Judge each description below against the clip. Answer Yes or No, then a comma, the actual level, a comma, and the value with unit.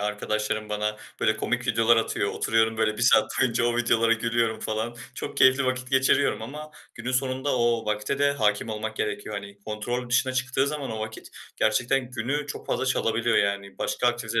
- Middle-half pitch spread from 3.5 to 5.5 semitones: No, average, 3.0 semitones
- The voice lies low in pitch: Yes, low, 115 Hz